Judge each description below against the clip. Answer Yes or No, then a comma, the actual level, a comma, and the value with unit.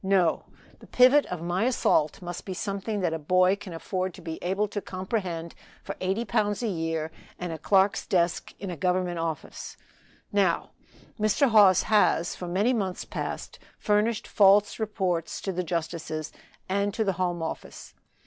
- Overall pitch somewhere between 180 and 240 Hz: Yes, medium, 185 Hz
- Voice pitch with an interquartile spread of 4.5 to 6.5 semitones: No, average, 3.2 semitones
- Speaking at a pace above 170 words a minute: No, average, 165 wpm